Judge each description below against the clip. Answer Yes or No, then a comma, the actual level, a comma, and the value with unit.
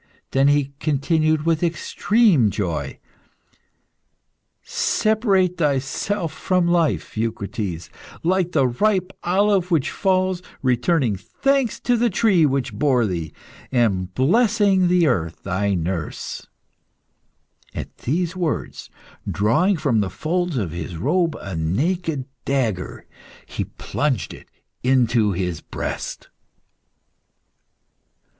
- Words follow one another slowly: Yes, slow, 105 wpm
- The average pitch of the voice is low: No, medium, 145 Hz